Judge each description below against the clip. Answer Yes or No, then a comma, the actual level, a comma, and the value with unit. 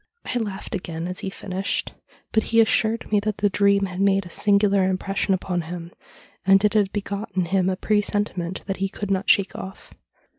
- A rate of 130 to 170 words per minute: No, average, 195 wpm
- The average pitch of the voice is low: No, high, 195 Hz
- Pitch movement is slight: Yes, narrow, 1.7 semitones